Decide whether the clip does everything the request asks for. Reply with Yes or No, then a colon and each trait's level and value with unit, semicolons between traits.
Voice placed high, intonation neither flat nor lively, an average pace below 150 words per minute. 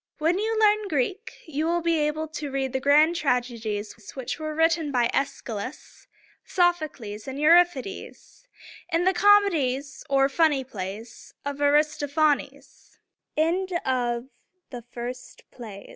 Yes: very high, 290 Hz; average, 5.0 semitones; average, 140 wpm